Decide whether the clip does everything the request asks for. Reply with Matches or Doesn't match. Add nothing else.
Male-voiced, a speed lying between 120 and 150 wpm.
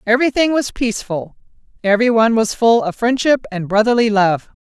Doesn't match